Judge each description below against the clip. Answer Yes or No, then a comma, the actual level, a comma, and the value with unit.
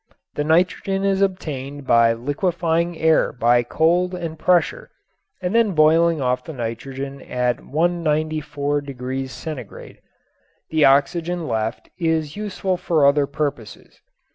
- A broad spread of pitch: No, average, 4.4 semitones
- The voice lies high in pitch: No, medium, 155 Hz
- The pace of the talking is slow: Yes, slow, 115 wpm